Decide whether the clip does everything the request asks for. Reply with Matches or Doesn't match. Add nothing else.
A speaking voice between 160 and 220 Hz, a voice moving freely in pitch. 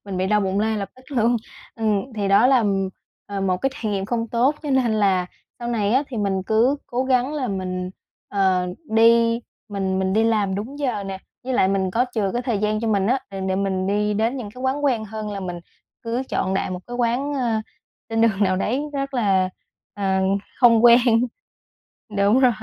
Doesn't match